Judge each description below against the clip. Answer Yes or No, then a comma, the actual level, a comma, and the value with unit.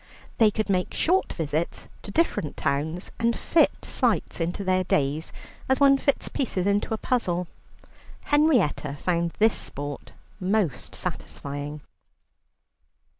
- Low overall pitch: No, medium, 185 Hz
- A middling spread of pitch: No, wide, 7.0 semitones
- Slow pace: Yes, slow, 125 wpm